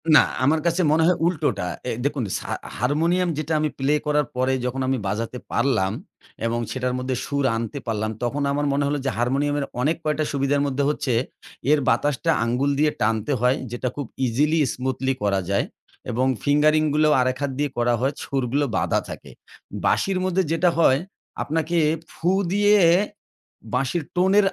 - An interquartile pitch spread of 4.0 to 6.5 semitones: No, average, 3.4 semitones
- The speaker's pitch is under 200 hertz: Yes, medium, 140 Hz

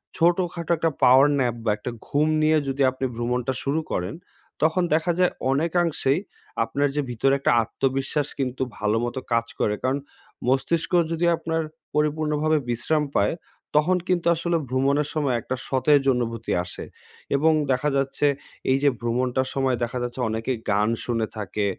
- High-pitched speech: No, low, 135 Hz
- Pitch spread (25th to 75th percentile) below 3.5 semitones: No, average, 4.2 semitones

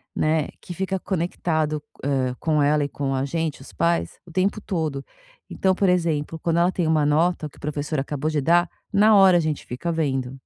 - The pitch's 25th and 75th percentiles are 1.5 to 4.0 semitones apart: Yes, average, 3.2 semitones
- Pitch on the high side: No, medium, 160 Hz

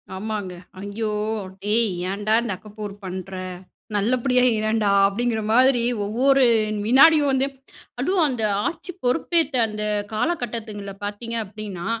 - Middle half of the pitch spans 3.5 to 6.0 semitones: Yes, average, 3.9 semitones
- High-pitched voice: Yes, high, 220 Hz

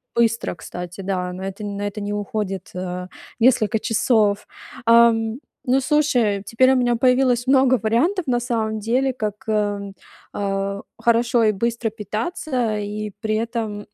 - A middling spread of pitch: Yes, average, 3.0 semitones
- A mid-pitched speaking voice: No, high, 220 Hz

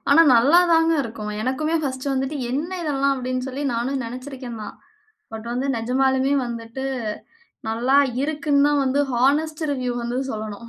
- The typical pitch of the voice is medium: No, very high, 265 Hz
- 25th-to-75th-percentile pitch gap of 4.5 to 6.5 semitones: No, average, 3.0 semitones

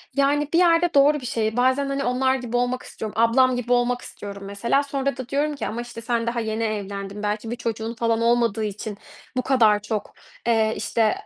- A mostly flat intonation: No, average, 3.1 semitones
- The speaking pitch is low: No, high, 235 Hz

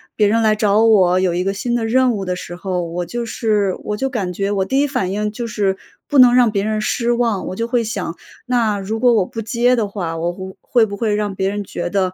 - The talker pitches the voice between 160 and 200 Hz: No, high, 210 Hz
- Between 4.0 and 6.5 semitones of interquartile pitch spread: No, average, 3.5 semitones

